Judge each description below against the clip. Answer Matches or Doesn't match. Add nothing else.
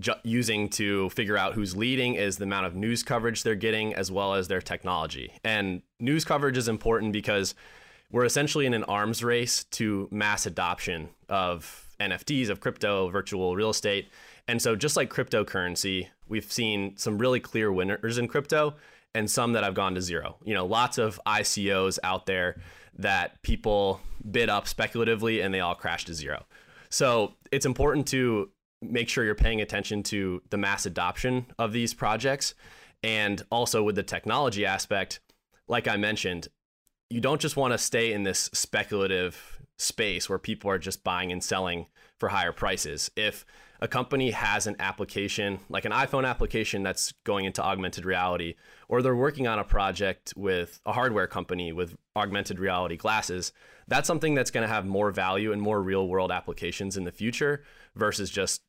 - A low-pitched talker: Matches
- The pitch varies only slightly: Doesn't match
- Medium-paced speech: Matches